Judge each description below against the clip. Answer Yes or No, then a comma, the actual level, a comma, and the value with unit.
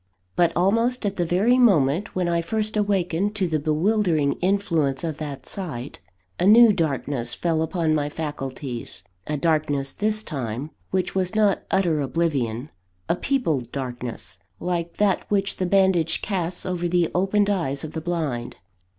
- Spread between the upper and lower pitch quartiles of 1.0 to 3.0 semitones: No, average, 5.2 semitones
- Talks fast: No, average, 155 wpm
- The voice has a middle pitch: Yes, medium, 170 Hz